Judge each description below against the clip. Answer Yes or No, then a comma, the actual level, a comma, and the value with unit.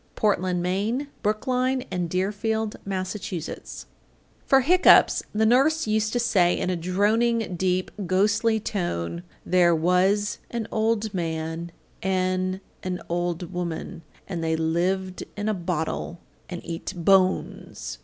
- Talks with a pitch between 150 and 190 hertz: Yes, medium, 185 Hz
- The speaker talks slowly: Yes, slow, 125 wpm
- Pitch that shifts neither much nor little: Yes, average, 3.6 semitones